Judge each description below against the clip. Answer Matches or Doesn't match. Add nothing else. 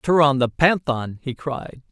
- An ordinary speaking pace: Matches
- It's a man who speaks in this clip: Matches